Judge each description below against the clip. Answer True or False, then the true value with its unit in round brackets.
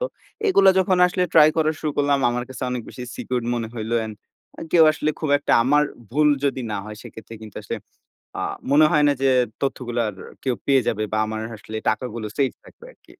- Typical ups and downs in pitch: True (4.8 semitones)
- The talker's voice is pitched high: False (130 Hz)